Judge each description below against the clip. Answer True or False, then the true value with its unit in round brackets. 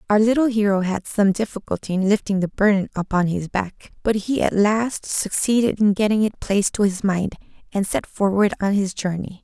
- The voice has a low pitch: False (200 Hz)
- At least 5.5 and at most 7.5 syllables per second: False (5.2 syllables/s)